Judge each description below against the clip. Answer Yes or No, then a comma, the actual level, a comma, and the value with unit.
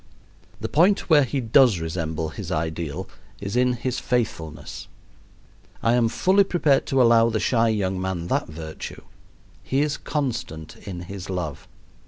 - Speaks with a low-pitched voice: Yes, low, 110 Hz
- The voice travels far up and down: Yes, wide, 7.5 semitones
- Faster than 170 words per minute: No, average, 150 wpm